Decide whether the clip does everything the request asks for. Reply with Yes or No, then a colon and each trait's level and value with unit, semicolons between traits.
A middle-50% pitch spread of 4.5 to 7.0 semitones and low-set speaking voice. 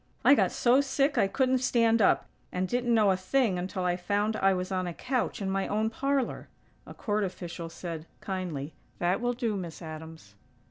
No: average, 5.2 semitones; high, 195 Hz